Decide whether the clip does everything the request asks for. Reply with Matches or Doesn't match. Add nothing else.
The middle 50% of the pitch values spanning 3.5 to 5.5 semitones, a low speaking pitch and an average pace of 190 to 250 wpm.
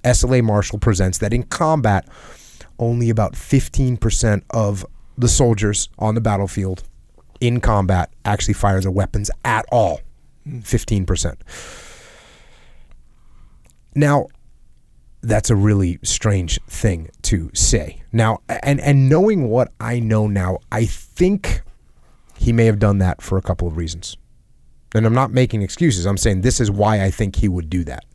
Doesn't match